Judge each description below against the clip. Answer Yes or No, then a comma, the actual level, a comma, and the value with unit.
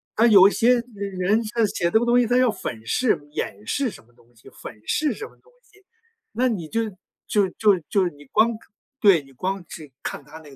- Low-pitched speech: No, high, 200 Hz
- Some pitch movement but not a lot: No, wide, 7.5 semitones